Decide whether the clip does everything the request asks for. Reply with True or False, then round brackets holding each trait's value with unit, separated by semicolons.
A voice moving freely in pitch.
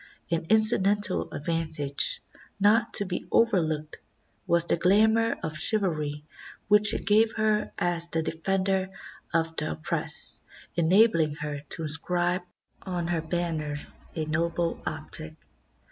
False (4.3 semitones)